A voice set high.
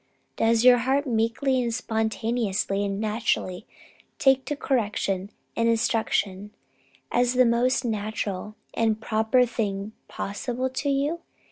Yes: high, 230 Hz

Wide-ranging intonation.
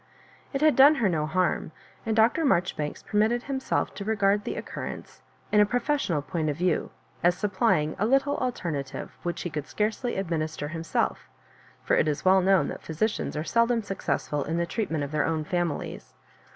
Yes: wide, 6.3 semitones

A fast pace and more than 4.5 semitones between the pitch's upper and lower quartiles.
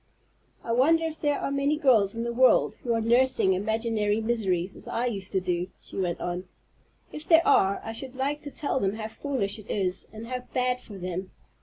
Yes: fast, 210 wpm; average, 5.0 semitones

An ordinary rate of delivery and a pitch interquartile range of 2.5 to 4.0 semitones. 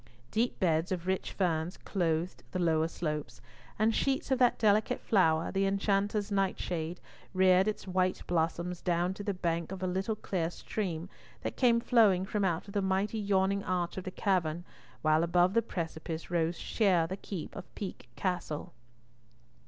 Yes: average, 170 wpm; average, 2.9 semitones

